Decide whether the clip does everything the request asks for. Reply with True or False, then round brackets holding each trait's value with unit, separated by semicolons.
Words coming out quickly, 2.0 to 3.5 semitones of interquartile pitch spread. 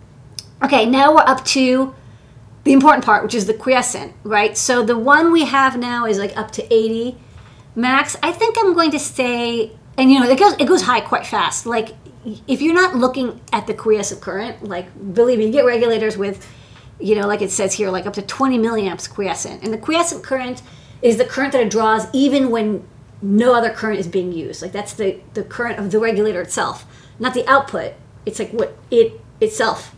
False (210 wpm; 4.2 semitones)